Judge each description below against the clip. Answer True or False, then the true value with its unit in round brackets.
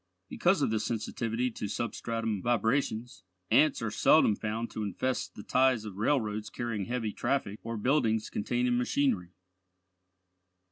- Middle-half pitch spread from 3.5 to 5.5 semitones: False (2.7 semitones)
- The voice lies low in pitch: True (115 Hz)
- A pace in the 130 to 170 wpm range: True (135 wpm)